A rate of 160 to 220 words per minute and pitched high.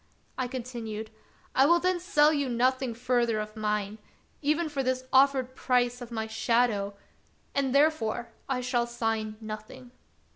No: average, 150 wpm; high, 245 Hz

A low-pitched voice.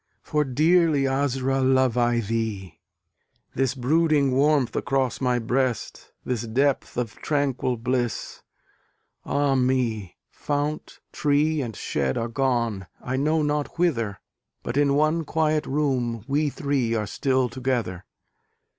Yes: low, 130 Hz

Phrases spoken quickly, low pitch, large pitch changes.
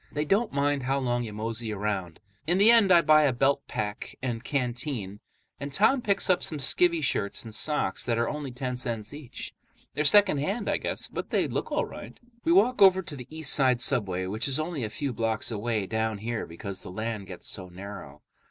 Yes: fast, 210 wpm; low, 125 Hz; wide, 6.0 semitones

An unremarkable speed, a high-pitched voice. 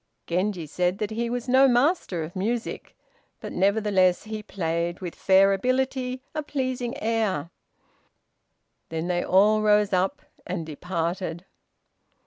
No: slow, 125 wpm; high, 200 Hz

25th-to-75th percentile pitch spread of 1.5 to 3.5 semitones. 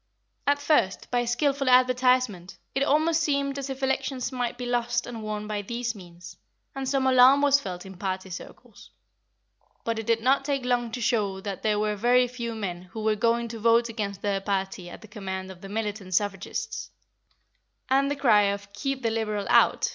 No: average, 4.2 semitones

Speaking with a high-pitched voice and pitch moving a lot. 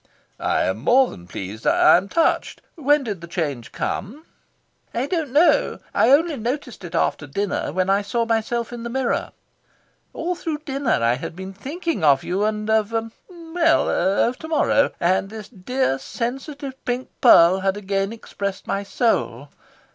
Yes: high, 220 Hz; wide, 6.4 semitones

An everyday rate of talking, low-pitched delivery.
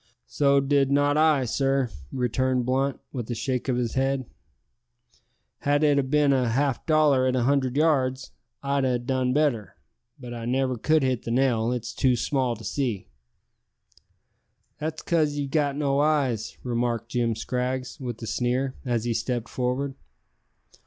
Yes: average, 160 wpm; low, 130 Hz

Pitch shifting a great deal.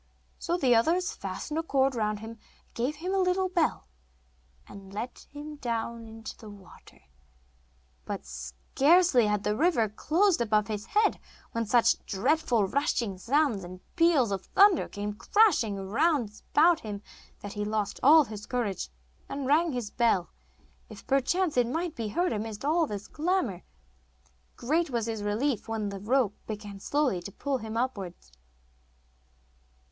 Yes: wide, 6.7 semitones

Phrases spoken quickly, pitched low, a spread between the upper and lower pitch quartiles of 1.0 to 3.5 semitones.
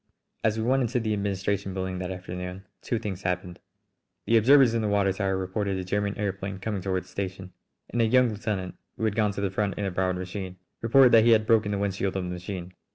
Yes: fast, 235 wpm; low, 100 Hz; average, 2.8 semitones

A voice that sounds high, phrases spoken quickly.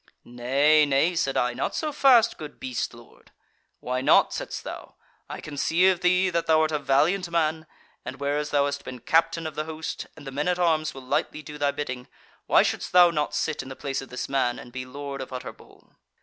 No: medium, 150 Hz; fast, 220 wpm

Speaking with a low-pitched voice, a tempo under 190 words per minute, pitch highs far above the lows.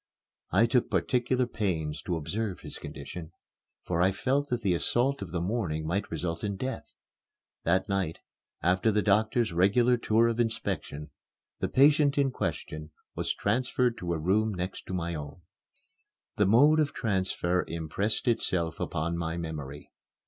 Yes: very low, 95 Hz; average, 150 wpm; wide, 5.9 semitones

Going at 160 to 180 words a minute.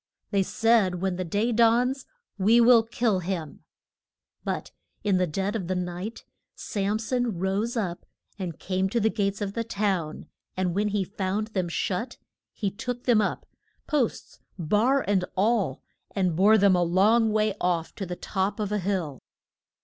Yes: average, 170 wpm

